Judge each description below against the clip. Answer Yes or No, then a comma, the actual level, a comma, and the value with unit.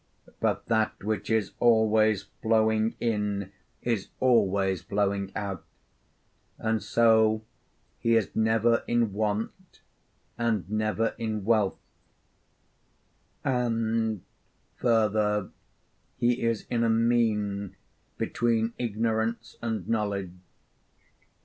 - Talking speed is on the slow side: Yes, slow, 90 wpm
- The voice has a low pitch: Yes, low, 110 Hz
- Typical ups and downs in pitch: No, narrow, 1.8 semitones